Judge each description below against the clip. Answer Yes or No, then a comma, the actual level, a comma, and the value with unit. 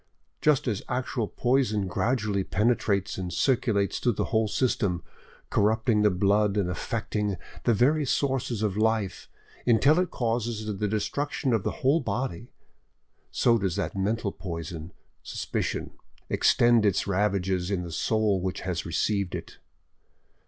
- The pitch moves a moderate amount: Yes, average, 3.7 semitones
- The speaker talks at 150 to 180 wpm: No, average, 140 wpm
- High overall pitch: No, low, 105 Hz